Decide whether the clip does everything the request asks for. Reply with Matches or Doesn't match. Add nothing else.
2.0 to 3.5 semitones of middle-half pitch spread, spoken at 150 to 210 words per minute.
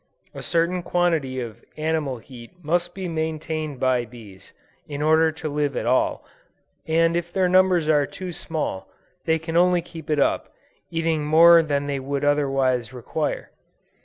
Matches